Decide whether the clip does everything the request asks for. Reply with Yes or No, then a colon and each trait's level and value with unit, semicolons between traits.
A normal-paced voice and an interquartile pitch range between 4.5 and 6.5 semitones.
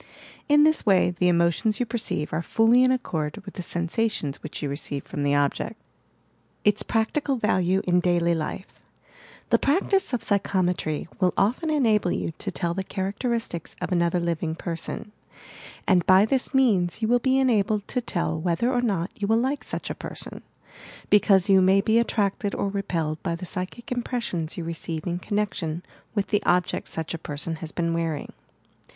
Yes: average, 180 wpm; average, 4.9 semitones